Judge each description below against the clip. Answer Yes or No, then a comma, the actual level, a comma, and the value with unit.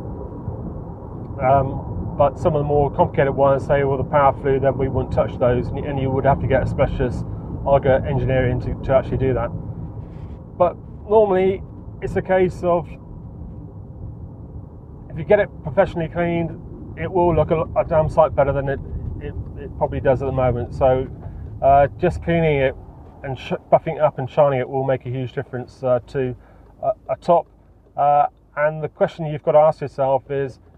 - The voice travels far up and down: No, average, 3.3 semitones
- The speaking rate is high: No, average, 185 wpm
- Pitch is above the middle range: No, low, 135 Hz